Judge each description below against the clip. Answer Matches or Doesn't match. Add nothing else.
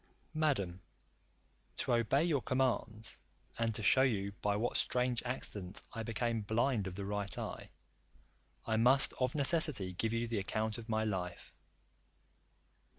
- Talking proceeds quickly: Doesn't match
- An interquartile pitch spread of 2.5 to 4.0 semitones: Matches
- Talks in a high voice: Doesn't match